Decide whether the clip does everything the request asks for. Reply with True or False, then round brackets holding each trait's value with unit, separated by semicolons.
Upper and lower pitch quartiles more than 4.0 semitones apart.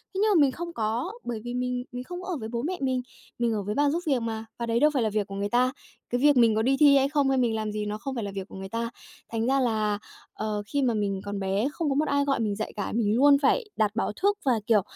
True (4.4 semitones)